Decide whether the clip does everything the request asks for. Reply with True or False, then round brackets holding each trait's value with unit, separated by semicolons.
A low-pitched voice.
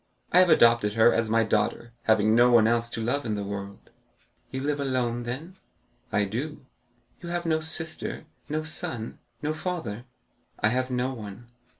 True (120 Hz)